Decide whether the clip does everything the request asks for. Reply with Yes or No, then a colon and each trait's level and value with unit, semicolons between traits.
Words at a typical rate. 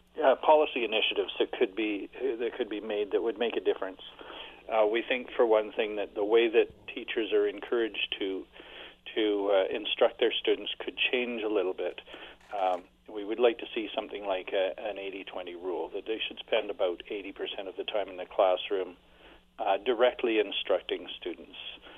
Yes: average, 185 wpm